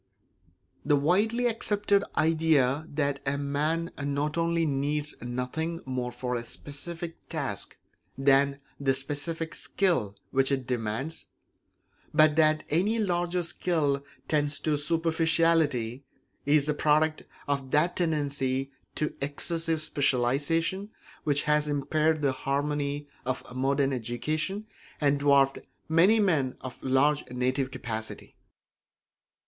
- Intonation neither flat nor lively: Yes, average, 3.1 semitones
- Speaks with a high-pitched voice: No, medium, 145 Hz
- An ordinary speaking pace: No, slow, 115 wpm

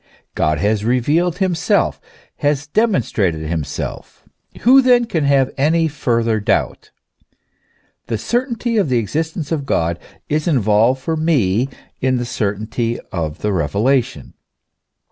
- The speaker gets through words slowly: Yes, slow, 125 wpm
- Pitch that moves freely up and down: Yes, wide, 7.2 semitones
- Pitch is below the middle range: Yes, low, 130 Hz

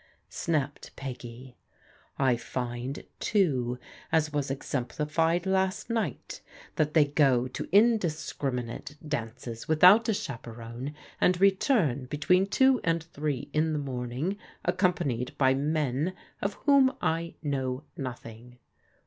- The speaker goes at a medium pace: No, slow, 120 wpm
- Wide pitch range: Yes, wide, 5.7 semitones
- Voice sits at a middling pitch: Yes, medium, 145 Hz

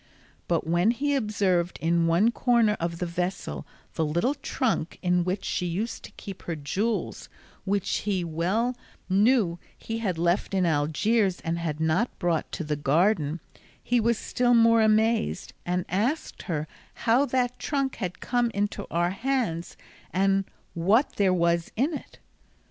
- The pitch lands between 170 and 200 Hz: Yes, high, 190 Hz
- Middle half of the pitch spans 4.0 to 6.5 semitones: Yes, average, 5.2 semitones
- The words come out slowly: No, average, 155 wpm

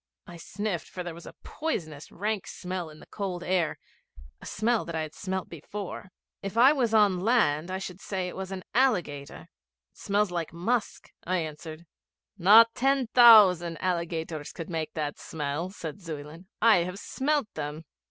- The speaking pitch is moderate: Yes, medium, 180 Hz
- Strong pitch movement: No, average, 4.3 semitones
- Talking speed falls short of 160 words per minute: No, average, 175 wpm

